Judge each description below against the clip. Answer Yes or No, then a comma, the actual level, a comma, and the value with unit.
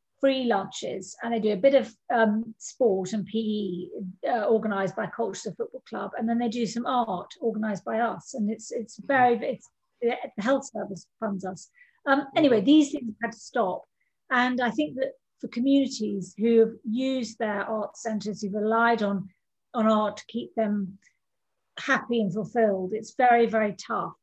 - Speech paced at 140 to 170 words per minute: No, average, 180 wpm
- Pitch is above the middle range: Yes, high, 225 Hz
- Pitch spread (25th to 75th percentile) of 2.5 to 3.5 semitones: Yes, average, 2.8 semitones